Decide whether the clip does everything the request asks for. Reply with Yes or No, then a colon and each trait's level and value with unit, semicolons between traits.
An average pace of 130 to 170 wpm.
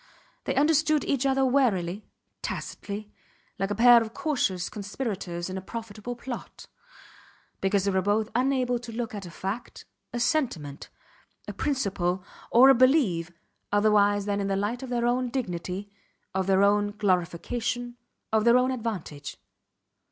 Yes: average, 150 wpm